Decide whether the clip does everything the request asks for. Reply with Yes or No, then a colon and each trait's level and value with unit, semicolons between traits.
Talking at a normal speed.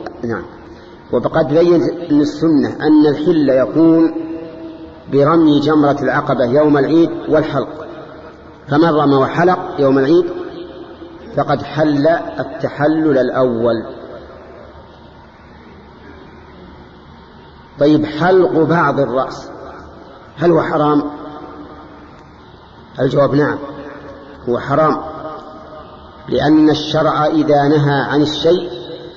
Yes: average, 80 wpm